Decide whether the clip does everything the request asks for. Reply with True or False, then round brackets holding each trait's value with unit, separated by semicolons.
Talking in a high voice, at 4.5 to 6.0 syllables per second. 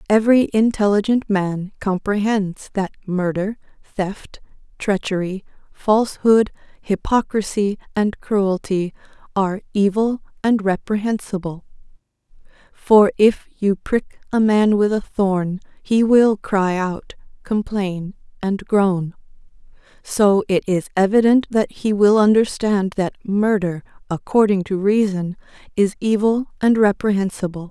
False (200 Hz; 4.0 syllables/s)